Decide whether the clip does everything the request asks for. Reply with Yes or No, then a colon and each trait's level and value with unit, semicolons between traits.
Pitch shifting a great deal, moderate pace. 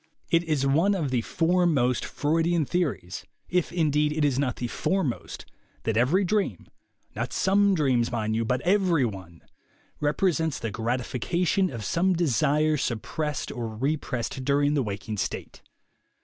Yes: wide, 6.0 semitones; average, 155 wpm